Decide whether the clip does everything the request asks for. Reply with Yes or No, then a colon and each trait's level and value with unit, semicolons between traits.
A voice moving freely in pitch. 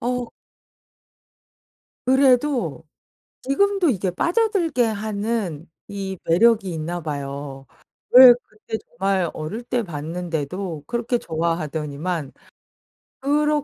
Yes: wide, 7.3 semitones